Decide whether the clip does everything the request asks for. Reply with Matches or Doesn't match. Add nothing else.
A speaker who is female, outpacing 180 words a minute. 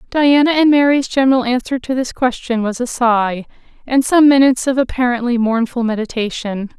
Doesn't match